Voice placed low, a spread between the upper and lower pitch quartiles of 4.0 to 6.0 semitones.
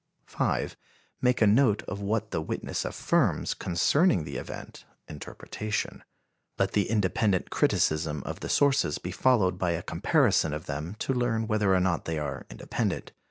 Yes: very low, 95 Hz; wide, 5.6 semitones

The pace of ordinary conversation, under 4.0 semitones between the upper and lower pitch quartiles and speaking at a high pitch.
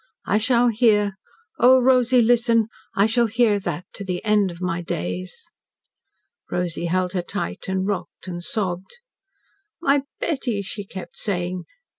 No: average, 145 wpm; average, 4.5 semitones; high, 205 Hz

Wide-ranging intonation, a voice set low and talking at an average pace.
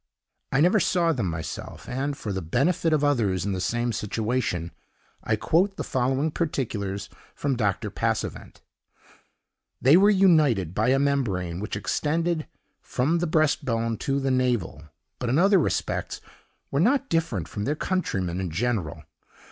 Yes: wide, 7.6 semitones; low, 130 Hz; average, 155 wpm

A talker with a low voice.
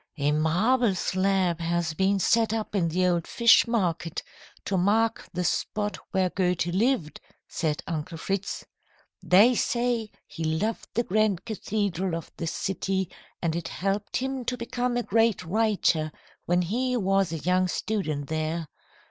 No: high, 190 Hz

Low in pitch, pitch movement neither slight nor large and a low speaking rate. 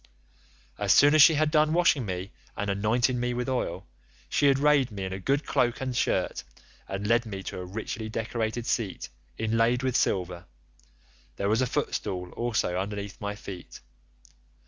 No: low, 115 Hz; average, 4.6 semitones; average, 170 wpm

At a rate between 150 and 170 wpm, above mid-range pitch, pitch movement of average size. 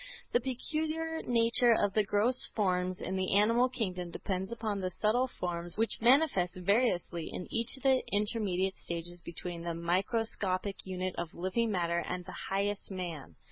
Yes: average, 160 wpm; high, 195 Hz; average, 4.4 semitones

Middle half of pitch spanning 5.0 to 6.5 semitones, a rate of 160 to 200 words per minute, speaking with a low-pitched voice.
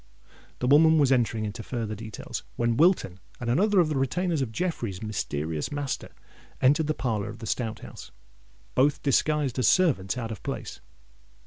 Yes: wide, 5.5 semitones; average, 165 wpm; low, 125 Hz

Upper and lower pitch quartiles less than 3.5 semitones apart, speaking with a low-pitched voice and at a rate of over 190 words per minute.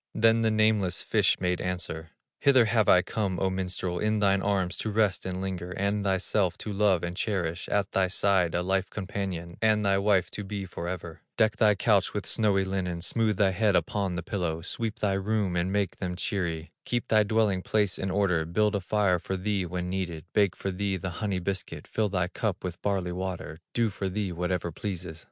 Yes: narrow, 2.6 semitones; very low, 95 Hz; fast, 205 wpm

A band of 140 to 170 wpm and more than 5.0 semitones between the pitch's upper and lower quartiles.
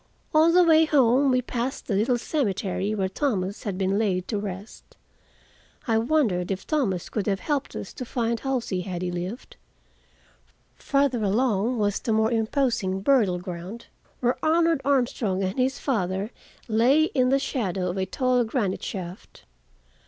Yes: average, 160 wpm; wide, 5.5 semitones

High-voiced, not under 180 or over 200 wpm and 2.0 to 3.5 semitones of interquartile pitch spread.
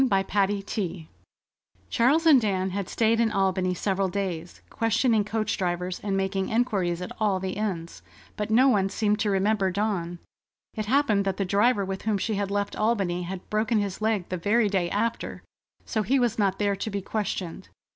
Yes: high, 200 Hz; average, 185 wpm; narrow, 2.4 semitones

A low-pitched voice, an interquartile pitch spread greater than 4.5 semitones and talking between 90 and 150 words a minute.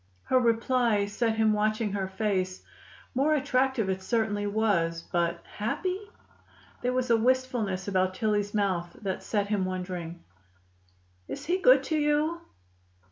No: high, 215 Hz; average, 5.0 semitones; slow, 135 wpm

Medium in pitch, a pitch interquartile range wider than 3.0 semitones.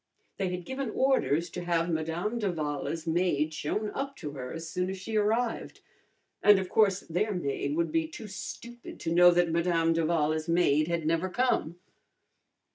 Yes: medium, 170 Hz; average, 3.5 semitones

